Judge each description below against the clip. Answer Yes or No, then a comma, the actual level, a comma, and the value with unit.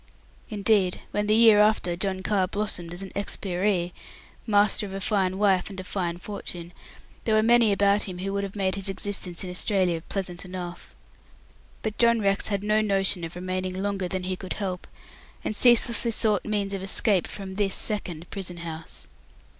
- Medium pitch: No, high, 195 Hz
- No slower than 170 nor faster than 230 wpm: Yes, average, 180 wpm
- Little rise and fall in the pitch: Yes, narrow, 2.2 semitones